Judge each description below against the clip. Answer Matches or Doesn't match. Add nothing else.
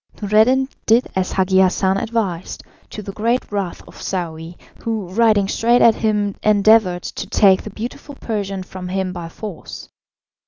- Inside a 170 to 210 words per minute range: Doesn't match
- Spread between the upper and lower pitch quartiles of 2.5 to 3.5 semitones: Matches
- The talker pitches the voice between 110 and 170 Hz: Doesn't match